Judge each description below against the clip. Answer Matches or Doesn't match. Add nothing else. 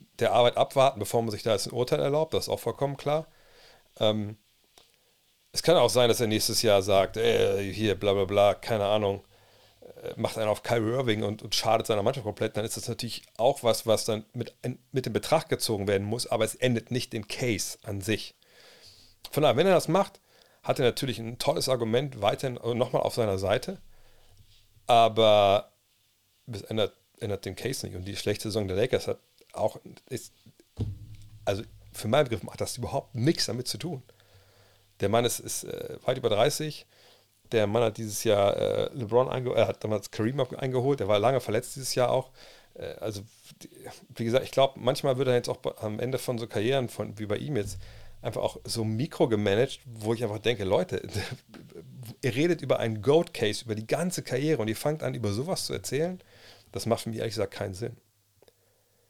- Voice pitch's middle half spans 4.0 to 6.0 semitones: Doesn't match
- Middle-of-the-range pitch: Doesn't match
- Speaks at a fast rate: Matches